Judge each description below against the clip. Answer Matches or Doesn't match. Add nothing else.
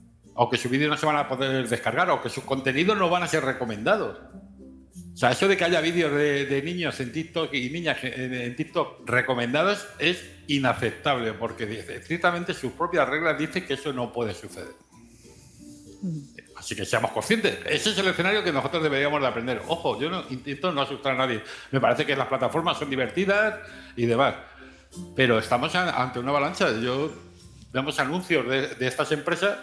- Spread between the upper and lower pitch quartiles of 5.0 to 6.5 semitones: Matches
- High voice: Doesn't match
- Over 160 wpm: Matches